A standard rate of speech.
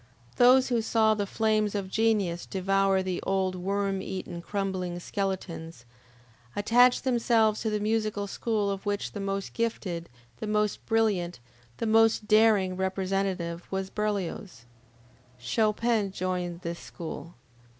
No: slow, 130 wpm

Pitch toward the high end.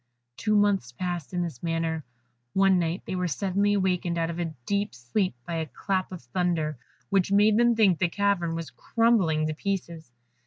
No: medium, 180 Hz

